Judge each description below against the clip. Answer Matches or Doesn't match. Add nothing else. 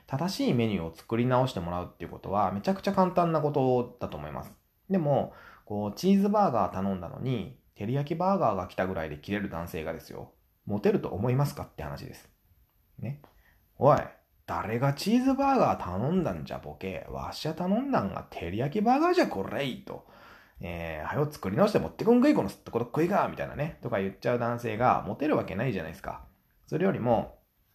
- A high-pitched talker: Doesn't match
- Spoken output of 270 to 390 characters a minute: Doesn't match